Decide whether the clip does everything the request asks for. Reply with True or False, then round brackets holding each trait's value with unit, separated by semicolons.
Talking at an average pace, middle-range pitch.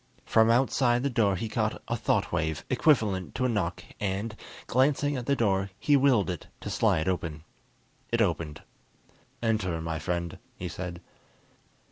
False (155 wpm; 100 Hz)